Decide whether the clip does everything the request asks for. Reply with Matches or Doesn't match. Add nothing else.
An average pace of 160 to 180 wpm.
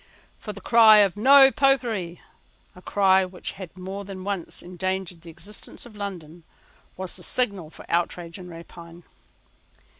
Doesn't match